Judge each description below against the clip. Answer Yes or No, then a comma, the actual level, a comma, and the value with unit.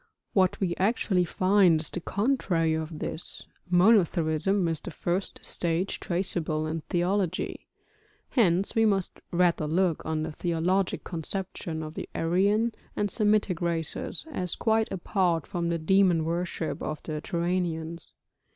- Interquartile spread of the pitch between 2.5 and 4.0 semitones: Yes, average, 2.9 semitones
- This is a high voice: No, medium, 175 Hz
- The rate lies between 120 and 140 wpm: Yes, slow, 135 wpm